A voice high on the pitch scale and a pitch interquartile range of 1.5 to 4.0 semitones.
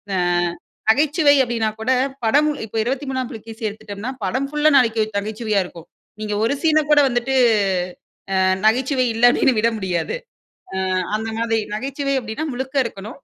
Yes: high, 235 Hz; average, 3.7 semitones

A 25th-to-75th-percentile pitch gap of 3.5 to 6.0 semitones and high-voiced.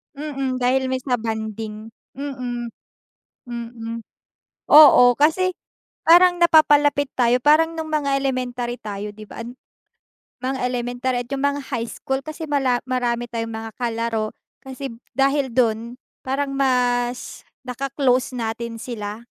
No: average, 2.9 semitones; very high, 250 Hz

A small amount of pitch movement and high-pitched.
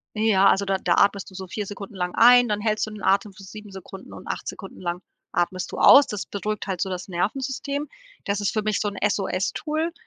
Yes: narrow, 2.1 semitones; high, 200 Hz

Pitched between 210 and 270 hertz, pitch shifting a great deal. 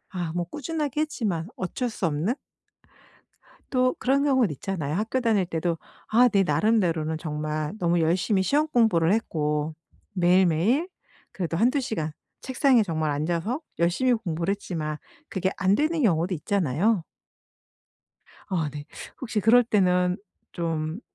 No: medium, 185 Hz; wide, 6.1 semitones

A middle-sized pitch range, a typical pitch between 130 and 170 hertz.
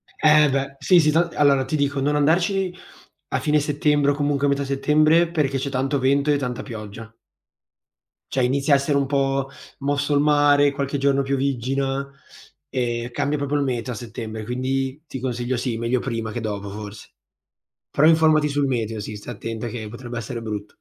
Yes: average, 3.1 semitones; low, 135 Hz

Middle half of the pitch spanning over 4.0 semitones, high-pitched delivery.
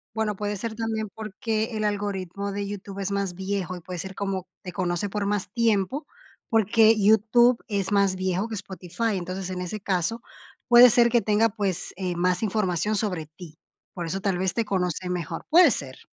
No: average, 2.9 semitones; high, 200 Hz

